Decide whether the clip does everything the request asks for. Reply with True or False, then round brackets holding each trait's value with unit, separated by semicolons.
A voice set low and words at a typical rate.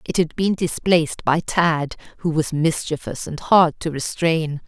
False (160 Hz; 165 wpm)